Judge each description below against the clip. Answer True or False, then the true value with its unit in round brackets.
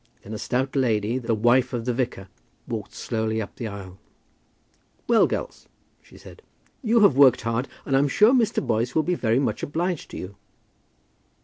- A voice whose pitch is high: False (125 Hz)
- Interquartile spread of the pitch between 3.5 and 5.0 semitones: True (4.4 semitones)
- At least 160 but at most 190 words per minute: True (185 wpm)